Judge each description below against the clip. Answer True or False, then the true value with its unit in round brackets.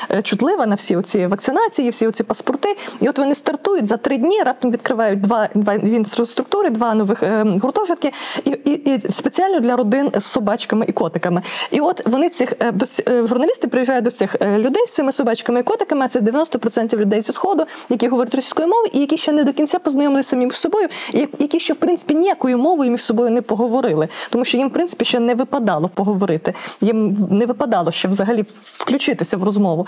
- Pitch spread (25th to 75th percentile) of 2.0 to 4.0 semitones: False (5.0 semitones)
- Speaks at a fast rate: True (195 wpm)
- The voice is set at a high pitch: True (250 Hz)